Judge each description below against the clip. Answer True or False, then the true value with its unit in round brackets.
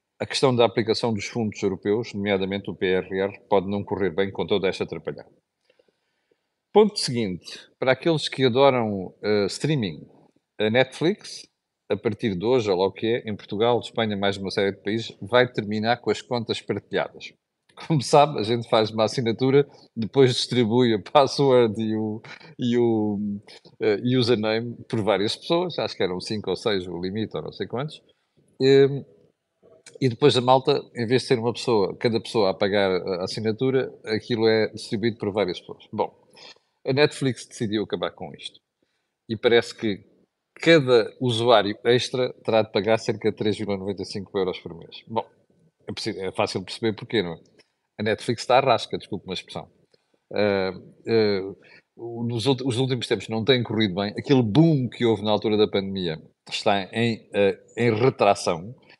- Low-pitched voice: True (115 Hz)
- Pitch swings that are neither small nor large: True (3.9 semitones)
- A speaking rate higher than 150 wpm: True (170 wpm)